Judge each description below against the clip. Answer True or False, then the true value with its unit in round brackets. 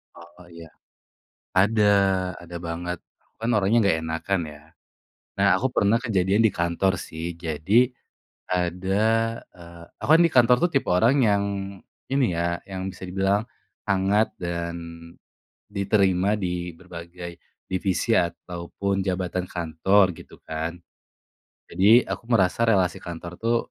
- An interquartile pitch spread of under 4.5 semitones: True (2.9 semitones)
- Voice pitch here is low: True (95 Hz)